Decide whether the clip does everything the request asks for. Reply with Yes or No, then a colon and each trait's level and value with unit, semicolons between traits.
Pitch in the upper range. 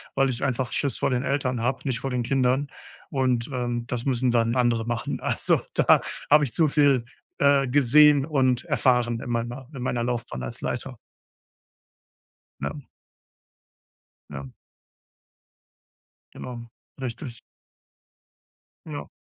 No: low, 125 Hz